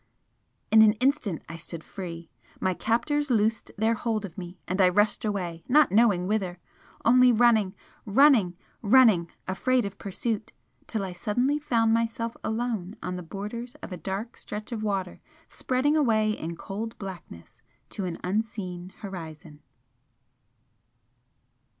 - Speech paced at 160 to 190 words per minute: No, average, 140 wpm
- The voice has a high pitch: Yes, high, 210 Hz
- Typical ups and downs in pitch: Yes, average, 4.1 semitones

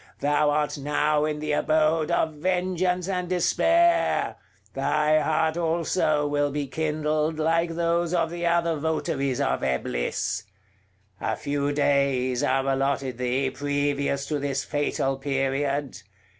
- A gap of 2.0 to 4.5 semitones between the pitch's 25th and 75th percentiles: Yes, average, 2.7 semitones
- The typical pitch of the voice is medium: Yes, medium, 150 Hz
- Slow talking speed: Yes, slow, 130 wpm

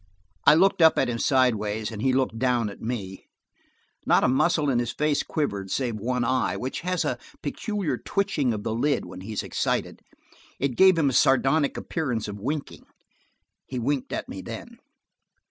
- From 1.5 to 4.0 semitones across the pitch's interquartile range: No, average, 5.0 semitones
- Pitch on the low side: Yes, low, 130 Hz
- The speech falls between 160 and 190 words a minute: Yes, average, 180 wpm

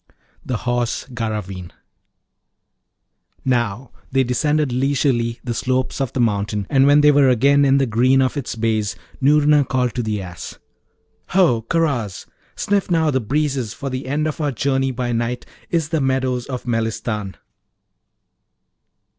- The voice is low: Yes, low, 130 Hz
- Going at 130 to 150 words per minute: Yes, average, 145 wpm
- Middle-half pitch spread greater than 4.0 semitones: No, average, 3.4 semitones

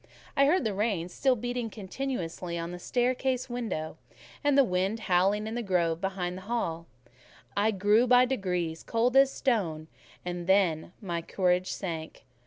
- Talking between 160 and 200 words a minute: Yes, average, 165 wpm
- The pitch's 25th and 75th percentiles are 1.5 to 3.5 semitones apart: No, wide, 5.5 semitones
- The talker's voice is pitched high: Yes, high, 195 Hz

